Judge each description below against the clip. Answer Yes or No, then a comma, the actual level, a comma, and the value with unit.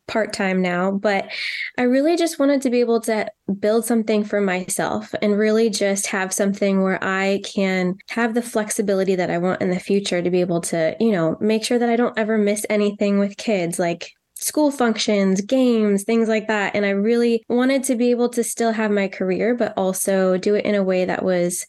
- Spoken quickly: Yes, fast, 215 wpm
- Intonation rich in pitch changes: No, average, 3.2 semitones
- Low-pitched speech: No, high, 210 Hz